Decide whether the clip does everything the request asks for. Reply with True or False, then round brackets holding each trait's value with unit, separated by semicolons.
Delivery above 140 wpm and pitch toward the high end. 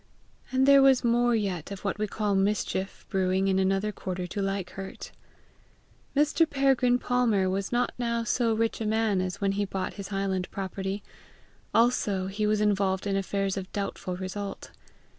True (170 wpm; 200 Hz)